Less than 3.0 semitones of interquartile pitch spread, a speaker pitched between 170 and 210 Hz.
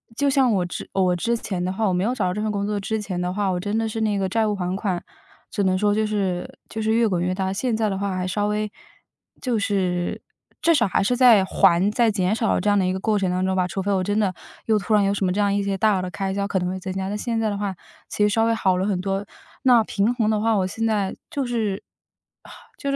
Yes: narrow, 2.6 semitones; high, 205 Hz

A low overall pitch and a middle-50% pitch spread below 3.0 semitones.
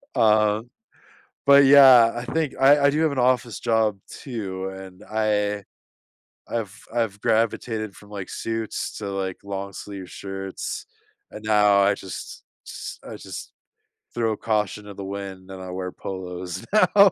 No: low, 105 Hz; average, 3.3 semitones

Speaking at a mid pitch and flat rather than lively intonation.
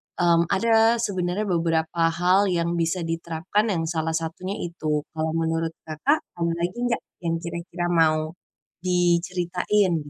Yes: medium, 170 Hz; narrow, 2.1 semitones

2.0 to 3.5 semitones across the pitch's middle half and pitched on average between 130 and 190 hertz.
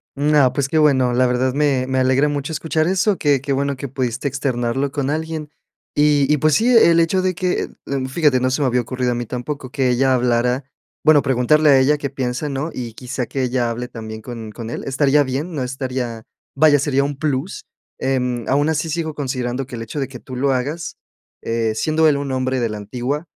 Yes: average, 3.0 semitones; low, 135 Hz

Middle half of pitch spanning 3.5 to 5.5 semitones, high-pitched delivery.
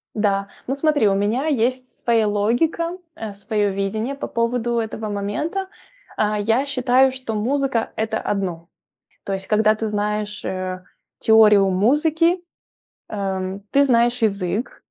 Yes: average, 4.0 semitones; high, 220 Hz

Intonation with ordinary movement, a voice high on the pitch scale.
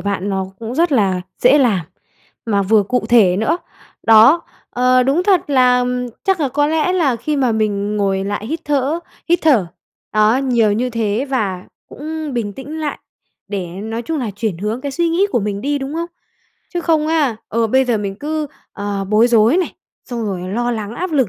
No: wide, 6.0 semitones; high, 240 Hz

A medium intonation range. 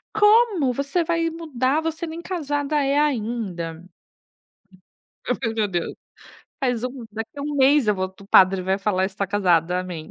No: wide, 7.7 semitones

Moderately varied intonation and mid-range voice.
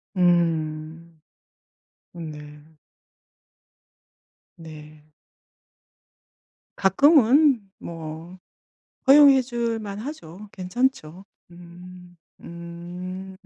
Yes: average, 4.7 semitones; medium, 180 Hz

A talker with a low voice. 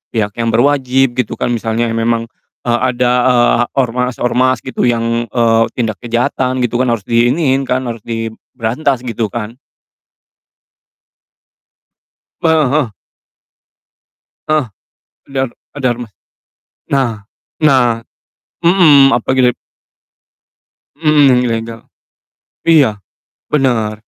Yes: low, 120 Hz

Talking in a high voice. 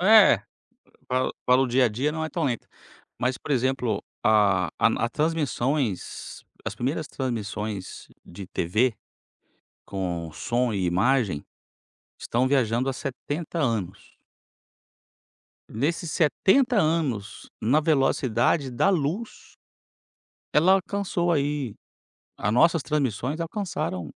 No: low, 130 Hz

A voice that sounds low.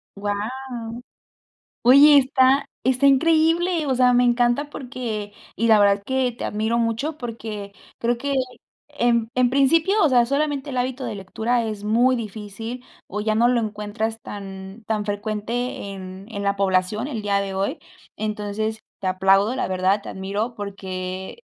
No: high, 225 Hz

